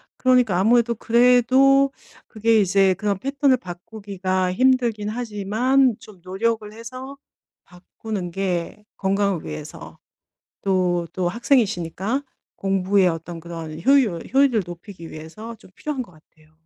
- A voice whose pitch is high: Yes, high, 205 Hz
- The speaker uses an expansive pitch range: No, average, 4.9 semitones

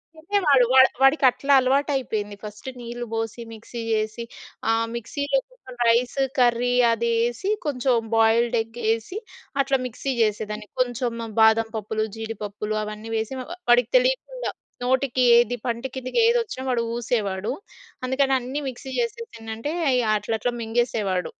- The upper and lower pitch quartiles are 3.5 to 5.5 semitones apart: No, average, 3.0 semitones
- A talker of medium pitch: No, high, 240 Hz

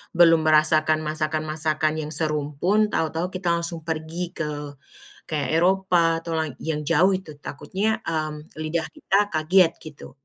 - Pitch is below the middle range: No, medium, 160 Hz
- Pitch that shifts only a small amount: Yes, narrow, 1.9 semitones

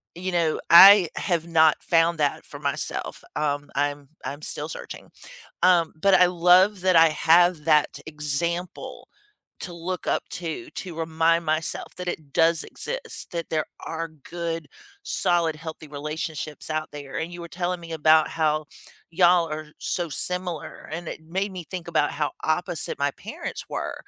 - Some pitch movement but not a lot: No, narrow, 2.2 semitones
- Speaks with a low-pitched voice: No, medium, 165 Hz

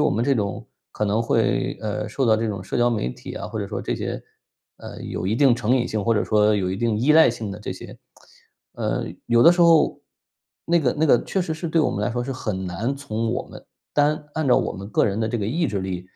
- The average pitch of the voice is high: No, low, 115 Hz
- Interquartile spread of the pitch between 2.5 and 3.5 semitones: No, average, 5.2 semitones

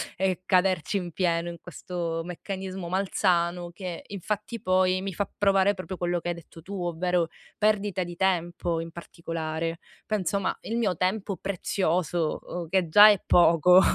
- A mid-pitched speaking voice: Yes, medium, 180 Hz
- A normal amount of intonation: No, narrow, 2.2 semitones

